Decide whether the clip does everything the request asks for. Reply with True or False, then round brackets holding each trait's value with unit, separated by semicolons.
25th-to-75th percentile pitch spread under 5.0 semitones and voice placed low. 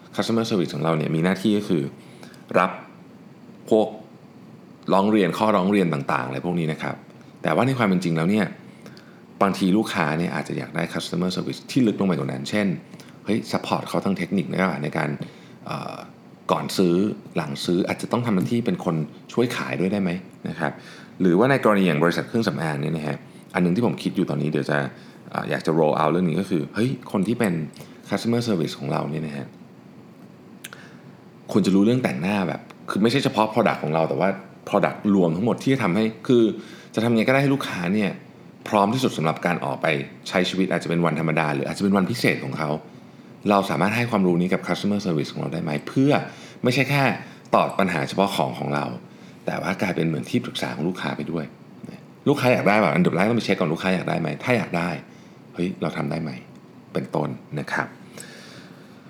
False (5.5 semitones; 90 Hz)